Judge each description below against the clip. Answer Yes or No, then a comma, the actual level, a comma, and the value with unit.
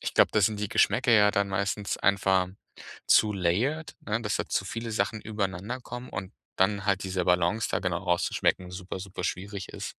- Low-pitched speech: Yes, low, 100 Hz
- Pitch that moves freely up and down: No, narrow, 2.4 semitones